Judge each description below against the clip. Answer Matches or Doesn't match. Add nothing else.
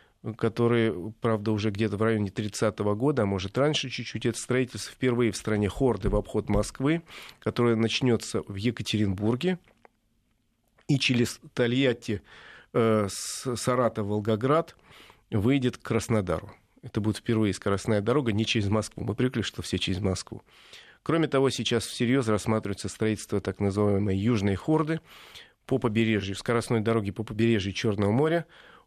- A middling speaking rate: Matches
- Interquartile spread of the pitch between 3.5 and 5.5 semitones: Doesn't match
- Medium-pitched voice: Doesn't match